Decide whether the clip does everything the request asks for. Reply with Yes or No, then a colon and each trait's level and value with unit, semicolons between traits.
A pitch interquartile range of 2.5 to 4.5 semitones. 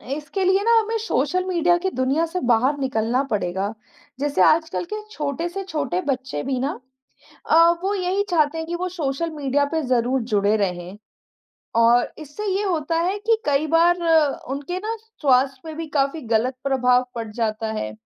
No: wide, 5.6 semitones